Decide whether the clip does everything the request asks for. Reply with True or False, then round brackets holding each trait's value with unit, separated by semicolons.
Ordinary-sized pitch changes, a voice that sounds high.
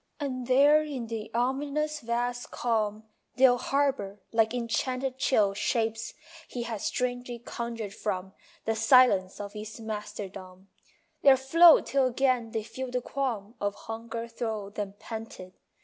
True (3.3 semitones; 235 Hz)